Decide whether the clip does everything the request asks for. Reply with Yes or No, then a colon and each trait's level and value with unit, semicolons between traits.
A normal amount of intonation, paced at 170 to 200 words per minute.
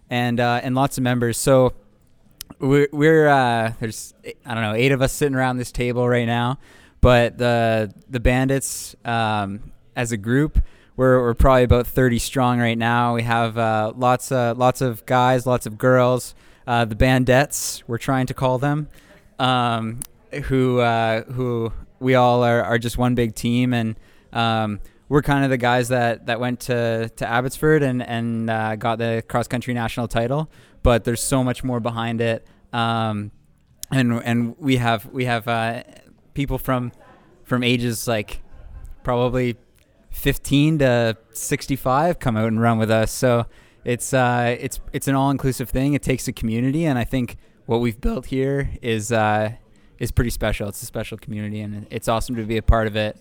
No: narrow, 2.1 semitones; average, 180 wpm